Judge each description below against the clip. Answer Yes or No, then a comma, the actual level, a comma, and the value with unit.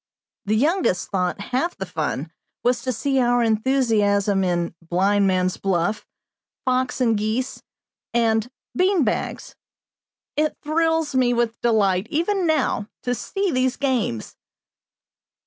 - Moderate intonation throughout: Yes, average, 4.9 semitones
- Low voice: No, high, 235 Hz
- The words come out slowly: Yes, slow, 120 wpm